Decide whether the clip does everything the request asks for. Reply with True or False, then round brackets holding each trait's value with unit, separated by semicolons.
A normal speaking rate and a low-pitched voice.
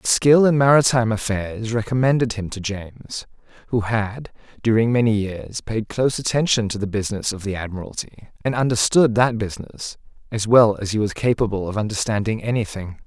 True (165 wpm; 110 Hz)